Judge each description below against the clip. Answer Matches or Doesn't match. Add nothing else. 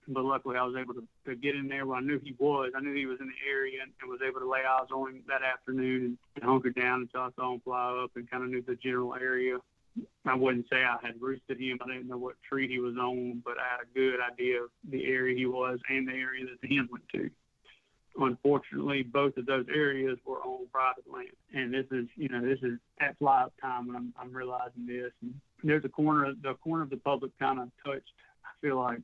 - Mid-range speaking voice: Doesn't match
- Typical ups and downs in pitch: Doesn't match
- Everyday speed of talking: Doesn't match